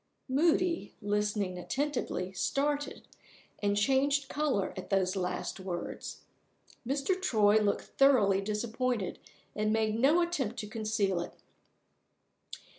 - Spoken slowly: Yes, slow, 110 wpm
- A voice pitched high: Yes, high, 220 Hz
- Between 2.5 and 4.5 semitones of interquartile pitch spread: No, wide, 5.4 semitones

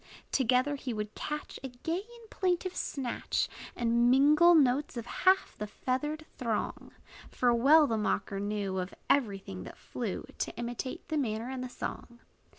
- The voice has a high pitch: Yes, very high, 250 Hz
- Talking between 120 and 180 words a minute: Yes, average, 160 wpm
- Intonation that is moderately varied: Yes, average, 4.8 semitones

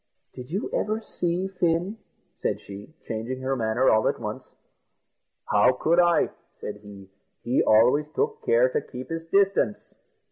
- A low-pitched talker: No, medium, 150 Hz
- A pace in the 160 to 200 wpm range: No, average, 150 wpm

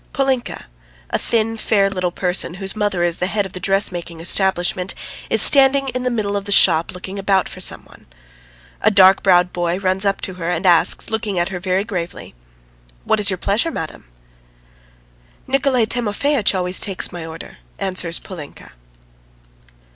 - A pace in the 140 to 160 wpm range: No, average, 170 wpm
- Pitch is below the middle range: No, high, 190 Hz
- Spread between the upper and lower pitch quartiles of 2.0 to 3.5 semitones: Yes, average, 2.9 semitones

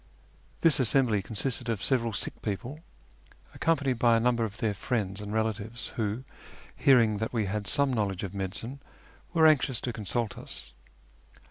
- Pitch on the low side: Yes, low, 115 Hz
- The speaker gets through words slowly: No, average, 160 wpm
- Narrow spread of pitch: No, average, 3.5 semitones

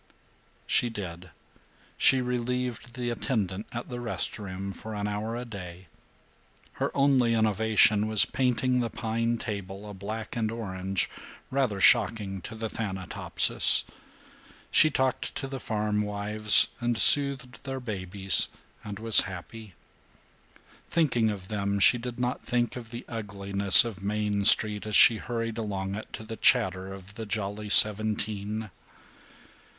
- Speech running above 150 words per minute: No, average, 140 wpm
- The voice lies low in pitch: Yes, low, 110 Hz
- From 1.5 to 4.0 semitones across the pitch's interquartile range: Yes, average, 3.0 semitones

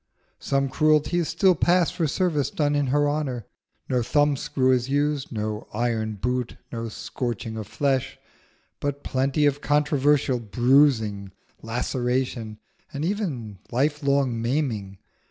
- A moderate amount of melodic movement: Yes, average, 3.9 semitones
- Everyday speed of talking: No, slow, 125 wpm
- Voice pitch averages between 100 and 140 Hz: Yes, low, 135 Hz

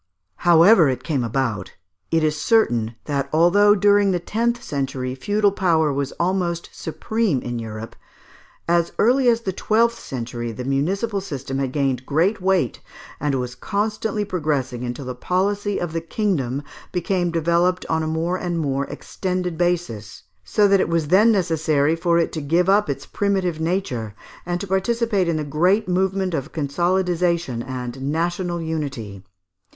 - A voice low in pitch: No, medium, 170 Hz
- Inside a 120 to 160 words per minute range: Yes, average, 155 wpm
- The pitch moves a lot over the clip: Yes, wide, 5.7 semitones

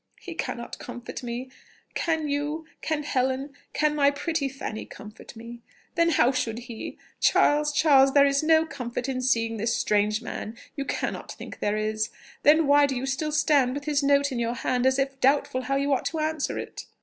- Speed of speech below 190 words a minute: No, average, 195 wpm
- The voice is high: Yes, very high, 275 Hz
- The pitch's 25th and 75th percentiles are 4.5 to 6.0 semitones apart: No, average, 3.5 semitones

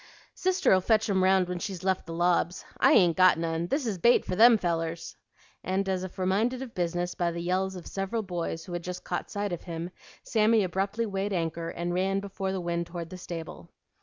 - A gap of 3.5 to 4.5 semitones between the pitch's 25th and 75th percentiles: No, narrow, 2.4 semitones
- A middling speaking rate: No, fast, 215 wpm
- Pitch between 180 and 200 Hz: Yes, medium, 185 Hz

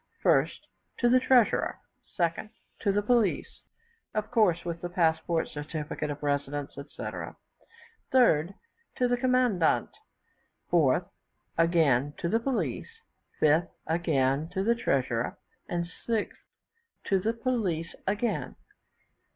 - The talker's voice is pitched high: No, medium, 175 Hz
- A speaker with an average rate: No, slow, 115 wpm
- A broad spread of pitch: Yes, wide, 6.8 semitones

